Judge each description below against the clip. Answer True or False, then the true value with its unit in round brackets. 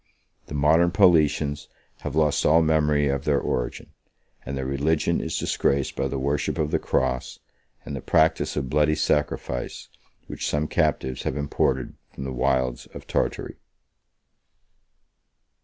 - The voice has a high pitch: False (75 Hz)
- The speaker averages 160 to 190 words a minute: False (140 wpm)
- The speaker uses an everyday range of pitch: False (2.2 semitones)